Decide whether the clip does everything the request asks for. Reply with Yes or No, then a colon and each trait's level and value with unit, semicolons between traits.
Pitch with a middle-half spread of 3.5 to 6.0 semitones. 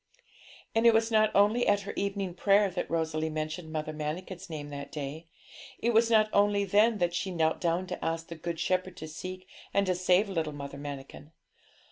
Yes: average, 4.3 semitones